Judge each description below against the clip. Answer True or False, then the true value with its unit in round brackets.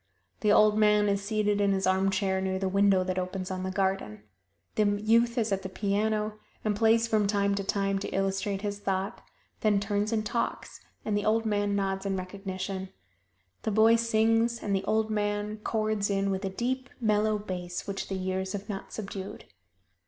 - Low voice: False (205 Hz)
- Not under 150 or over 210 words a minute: True (190 wpm)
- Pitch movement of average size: False (1.8 semitones)